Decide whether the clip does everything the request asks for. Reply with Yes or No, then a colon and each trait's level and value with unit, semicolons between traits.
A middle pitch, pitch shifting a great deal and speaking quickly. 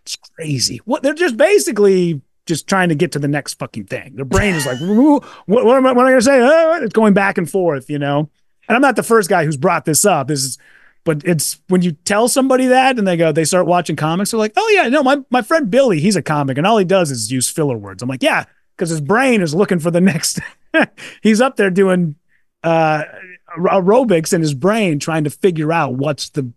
Yes: medium, 180 Hz; wide, 6.2 semitones; fast, 235 wpm